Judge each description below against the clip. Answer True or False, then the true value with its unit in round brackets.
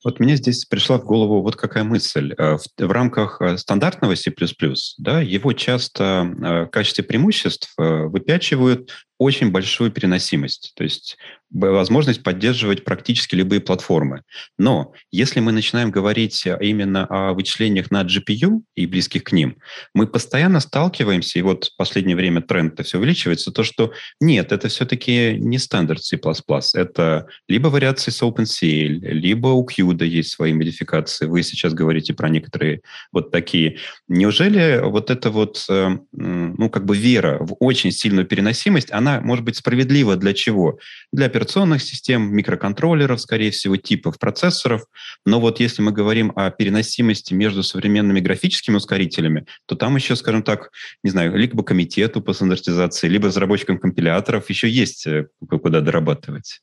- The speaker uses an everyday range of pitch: True (5.0 semitones)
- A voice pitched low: True (105 Hz)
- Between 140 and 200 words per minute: True (145 wpm)